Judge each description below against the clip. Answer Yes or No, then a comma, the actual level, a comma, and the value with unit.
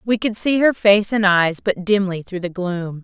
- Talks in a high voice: Yes, high, 195 Hz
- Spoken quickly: Yes, fast, 235 wpm